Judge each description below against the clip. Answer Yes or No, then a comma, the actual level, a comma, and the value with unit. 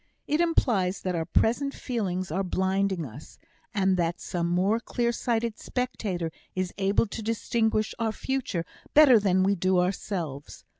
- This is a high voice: Yes, high, 195 Hz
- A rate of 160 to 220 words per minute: No, average, 150 wpm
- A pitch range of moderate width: Yes, average, 4.2 semitones